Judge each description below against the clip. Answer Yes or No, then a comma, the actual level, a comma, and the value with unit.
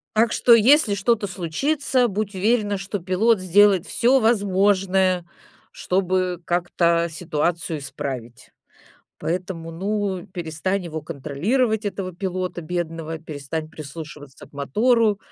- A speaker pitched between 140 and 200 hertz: Yes, medium, 185 Hz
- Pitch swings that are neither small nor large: Yes, average, 4.0 semitones